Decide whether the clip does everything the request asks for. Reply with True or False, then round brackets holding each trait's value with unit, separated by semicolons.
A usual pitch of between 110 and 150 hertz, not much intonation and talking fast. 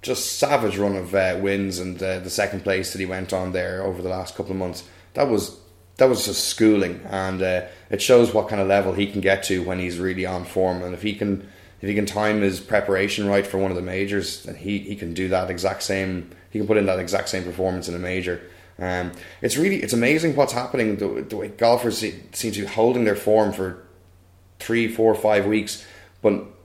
False (95 Hz; 2.3 semitones; 235 wpm)